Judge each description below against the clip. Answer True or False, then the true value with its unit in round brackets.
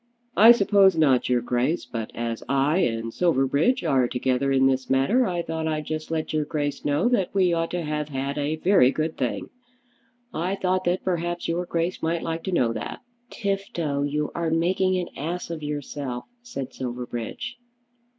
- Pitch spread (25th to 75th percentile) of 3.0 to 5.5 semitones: True (4.8 semitones)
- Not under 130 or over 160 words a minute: False (180 wpm)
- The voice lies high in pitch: False (155 Hz)